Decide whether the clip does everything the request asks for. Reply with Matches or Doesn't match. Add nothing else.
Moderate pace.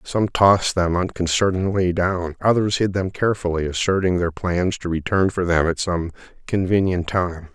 Matches